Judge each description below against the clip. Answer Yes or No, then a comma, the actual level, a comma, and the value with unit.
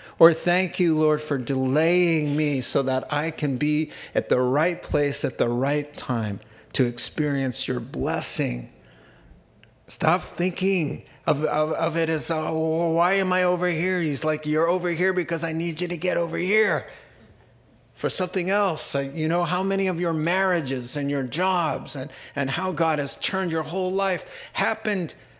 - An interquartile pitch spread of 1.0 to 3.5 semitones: No, average, 4.3 semitones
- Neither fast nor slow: Yes, average, 170 wpm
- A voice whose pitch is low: No, medium, 160 Hz